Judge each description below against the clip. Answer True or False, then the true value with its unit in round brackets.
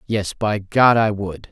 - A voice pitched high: False (105 Hz)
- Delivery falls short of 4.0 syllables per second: True (3.7 syllables/s)